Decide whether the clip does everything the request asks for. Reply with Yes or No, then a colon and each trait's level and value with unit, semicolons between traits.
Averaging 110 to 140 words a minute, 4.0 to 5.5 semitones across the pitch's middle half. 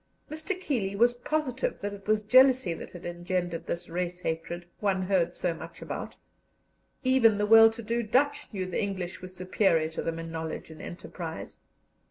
No: average, 180 wpm; average, 4.6 semitones